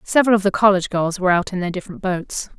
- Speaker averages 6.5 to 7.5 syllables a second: Yes, 7.4 syllables/s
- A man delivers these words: No, female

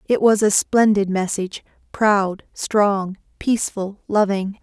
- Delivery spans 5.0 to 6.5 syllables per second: No, 3.9 syllables/s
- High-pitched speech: Yes, high, 200 Hz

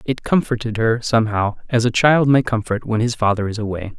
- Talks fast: Yes, fast, 210 wpm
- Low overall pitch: Yes, low, 115 Hz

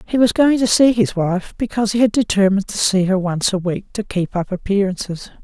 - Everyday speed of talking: No, fast, 230 wpm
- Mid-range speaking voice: No, high, 200 Hz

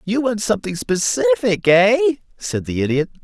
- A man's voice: Yes, male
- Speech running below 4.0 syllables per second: No, 5.0 syllables/s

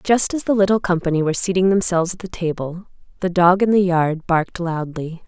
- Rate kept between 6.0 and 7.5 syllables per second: No, 5.7 syllables/s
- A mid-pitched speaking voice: Yes, medium, 180 Hz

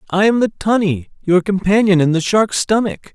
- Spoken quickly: No, average, 190 wpm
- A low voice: No, high, 190 Hz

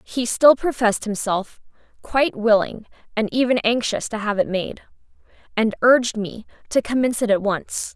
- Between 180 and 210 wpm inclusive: No, average, 160 wpm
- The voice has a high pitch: Yes, high, 225 Hz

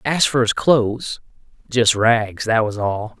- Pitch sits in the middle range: No, low, 115 Hz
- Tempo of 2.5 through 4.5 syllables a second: Yes, 3.9 syllables/s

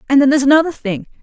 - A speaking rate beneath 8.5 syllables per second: No, 8.9 syllables/s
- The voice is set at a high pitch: Yes, very high, 275 Hz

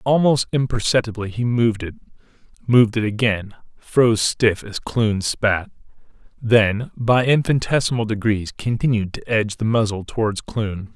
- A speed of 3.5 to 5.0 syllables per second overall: Yes, 4.9 syllables/s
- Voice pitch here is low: Yes, low, 110 Hz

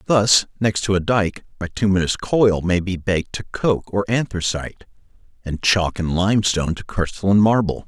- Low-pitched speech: Yes, very low, 95 Hz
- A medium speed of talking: Yes, average, 160 wpm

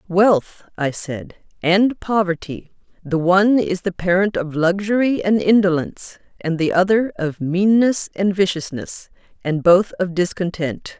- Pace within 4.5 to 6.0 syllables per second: No, 4.2 syllables/s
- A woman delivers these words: Yes, female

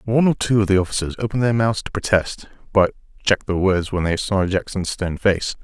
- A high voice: No, low, 100 Hz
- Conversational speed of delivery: No, fast, 225 wpm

